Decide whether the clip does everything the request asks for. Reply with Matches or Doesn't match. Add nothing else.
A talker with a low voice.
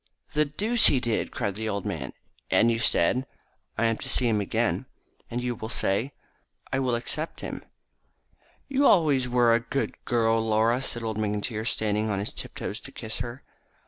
Matches